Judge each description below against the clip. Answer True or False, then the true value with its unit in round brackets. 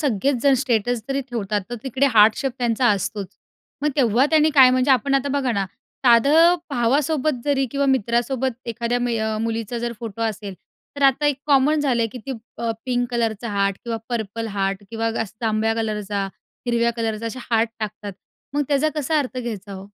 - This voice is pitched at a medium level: False (235 Hz)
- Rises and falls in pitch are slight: False (3.4 semitones)